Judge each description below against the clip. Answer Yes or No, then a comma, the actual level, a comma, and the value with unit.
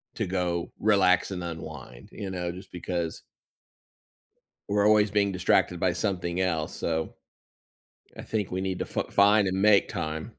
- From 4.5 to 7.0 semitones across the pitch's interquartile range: No, narrow, 2.6 semitones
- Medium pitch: No, very low, 90 Hz